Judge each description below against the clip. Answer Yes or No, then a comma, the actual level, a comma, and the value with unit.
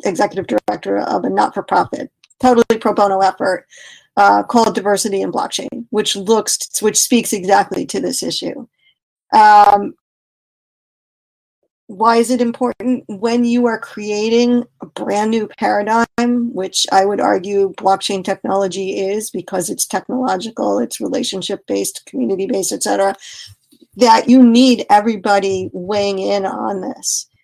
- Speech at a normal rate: No, slow, 130 wpm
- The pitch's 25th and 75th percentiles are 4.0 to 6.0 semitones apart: No, average, 3.5 semitones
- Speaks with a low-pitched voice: No, high, 215 Hz